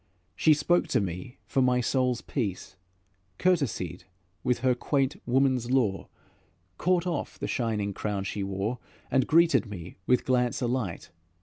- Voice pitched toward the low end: Yes, low, 125 Hz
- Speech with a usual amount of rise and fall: Yes, average, 5.0 semitones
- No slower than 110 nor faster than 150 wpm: Yes, average, 140 wpm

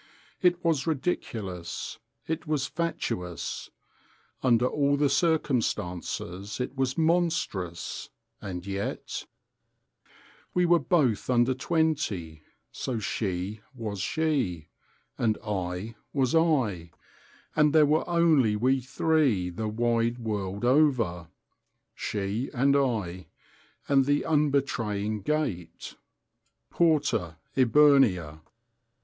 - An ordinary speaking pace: No, slow, 95 wpm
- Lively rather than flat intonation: Yes, wide, 7.2 semitones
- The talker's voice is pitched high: No, low, 125 Hz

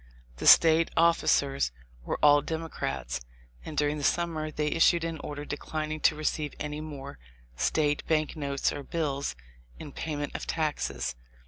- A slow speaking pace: No, average, 145 wpm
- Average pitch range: No, narrow, 1.8 semitones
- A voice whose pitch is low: No, medium, 150 Hz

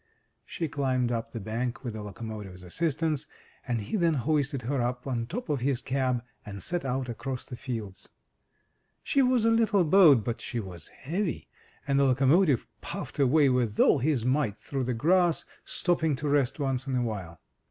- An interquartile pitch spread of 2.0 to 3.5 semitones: No, average, 4.5 semitones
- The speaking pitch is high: No, low, 130 Hz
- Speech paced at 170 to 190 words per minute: Yes, average, 185 wpm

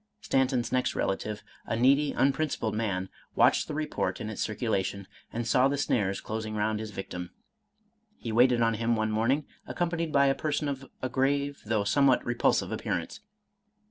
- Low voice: Yes, low, 120 Hz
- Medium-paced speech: Yes, average, 170 wpm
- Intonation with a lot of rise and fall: No, average, 4.3 semitones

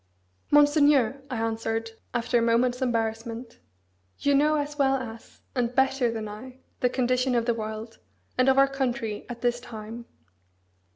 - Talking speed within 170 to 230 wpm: No, average, 155 wpm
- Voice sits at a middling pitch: No, high, 245 Hz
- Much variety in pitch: No, average, 2.8 semitones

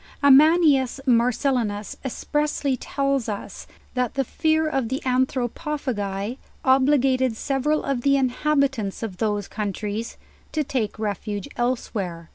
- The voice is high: Yes, very high, 255 Hz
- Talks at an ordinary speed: No, slow, 120 wpm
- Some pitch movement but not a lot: Yes, average, 4.2 semitones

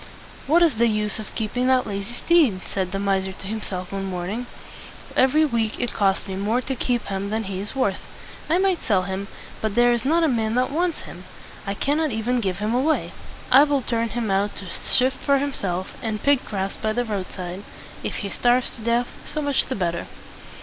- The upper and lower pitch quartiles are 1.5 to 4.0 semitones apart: No, average, 4.7 semitones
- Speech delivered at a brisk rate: Yes, fast, 210 wpm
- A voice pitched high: Yes, high, 225 Hz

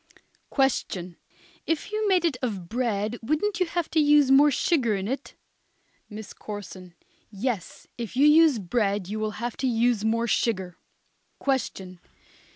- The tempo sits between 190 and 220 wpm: No, average, 150 wpm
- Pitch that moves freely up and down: Yes, wide, 6.0 semitones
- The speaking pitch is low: No, high, 235 Hz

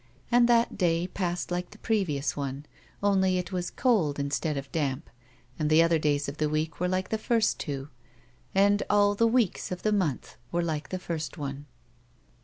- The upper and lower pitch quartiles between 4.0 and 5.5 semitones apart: Yes, average, 5.2 semitones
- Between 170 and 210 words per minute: Yes, average, 190 wpm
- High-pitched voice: No, medium, 175 Hz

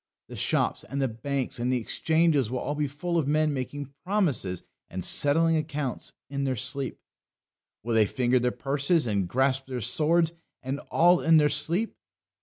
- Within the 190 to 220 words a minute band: No, average, 175 wpm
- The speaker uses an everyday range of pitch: Yes, average, 3.7 semitones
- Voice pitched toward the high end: No, medium, 140 Hz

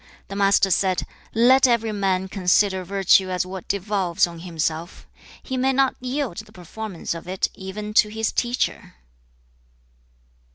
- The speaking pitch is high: Yes, high, 195 Hz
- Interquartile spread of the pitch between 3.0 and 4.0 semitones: Yes, average, 3.3 semitones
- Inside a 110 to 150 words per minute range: Yes, average, 140 wpm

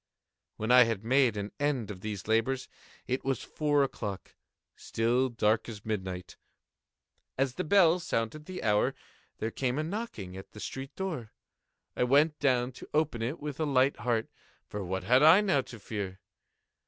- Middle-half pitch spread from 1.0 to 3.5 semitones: No, average, 5.1 semitones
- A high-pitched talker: No, low, 125 Hz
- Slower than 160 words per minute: No, average, 165 wpm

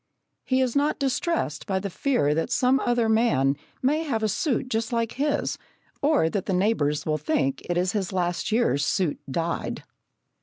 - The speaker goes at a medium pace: Yes, average, 180 wpm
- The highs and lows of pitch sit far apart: Yes, wide, 7.2 semitones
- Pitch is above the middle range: Yes, high, 220 Hz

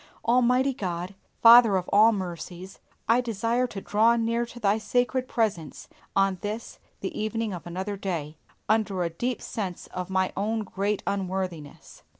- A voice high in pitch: Yes, high, 205 Hz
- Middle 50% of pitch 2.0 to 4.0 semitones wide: Yes, average, 3.7 semitones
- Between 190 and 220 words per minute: No, average, 155 wpm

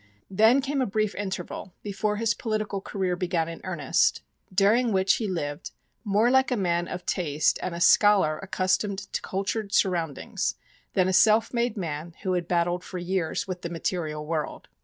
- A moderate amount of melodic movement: Yes, average, 3.5 semitones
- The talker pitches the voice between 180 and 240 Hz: Yes, high, 190 Hz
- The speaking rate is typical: Yes, average, 175 wpm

